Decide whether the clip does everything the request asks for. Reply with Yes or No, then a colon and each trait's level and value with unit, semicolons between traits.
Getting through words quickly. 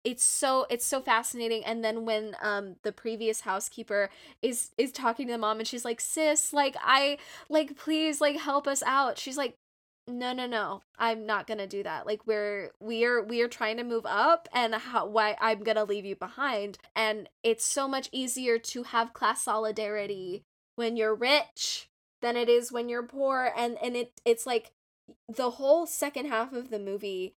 No: average, 195 wpm